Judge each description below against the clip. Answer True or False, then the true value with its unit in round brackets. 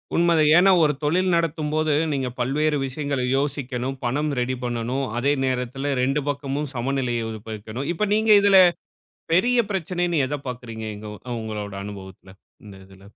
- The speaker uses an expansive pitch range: False (4.2 semitones)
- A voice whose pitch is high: False (135 Hz)